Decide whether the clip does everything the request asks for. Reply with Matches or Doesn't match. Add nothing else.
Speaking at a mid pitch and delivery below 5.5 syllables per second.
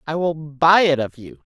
Matches